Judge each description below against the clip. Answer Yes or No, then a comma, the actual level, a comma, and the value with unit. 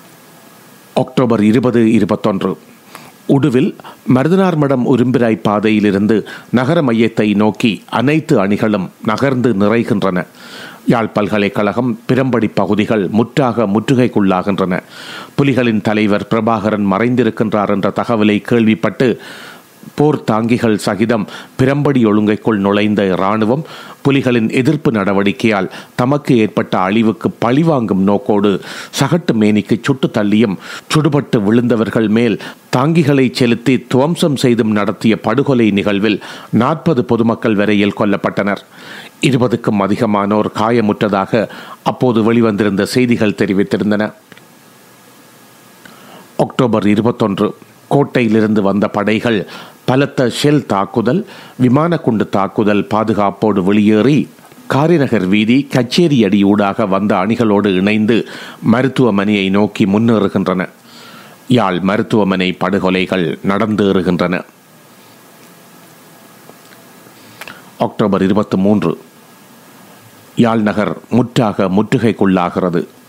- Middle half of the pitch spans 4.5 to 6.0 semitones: No, average, 3.2 semitones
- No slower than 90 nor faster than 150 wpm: No, average, 80 wpm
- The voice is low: Yes, low, 110 Hz